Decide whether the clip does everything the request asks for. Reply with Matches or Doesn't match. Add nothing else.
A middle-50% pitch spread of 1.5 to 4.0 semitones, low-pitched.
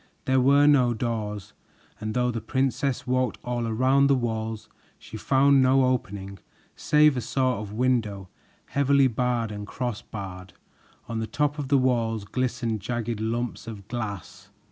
Matches